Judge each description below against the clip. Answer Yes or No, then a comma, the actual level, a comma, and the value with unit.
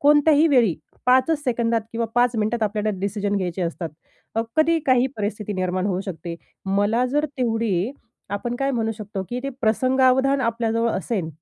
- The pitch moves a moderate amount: Yes, average, 3.9 semitones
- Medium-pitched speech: No, high, 225 Hz